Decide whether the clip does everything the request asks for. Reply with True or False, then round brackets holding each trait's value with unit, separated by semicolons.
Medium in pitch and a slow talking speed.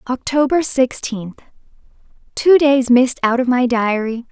False (250 Hz; 110 wpm)